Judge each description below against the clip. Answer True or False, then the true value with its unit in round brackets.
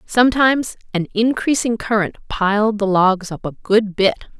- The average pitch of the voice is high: True (215 Hz)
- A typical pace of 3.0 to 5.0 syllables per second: True (4.9 syllables/s)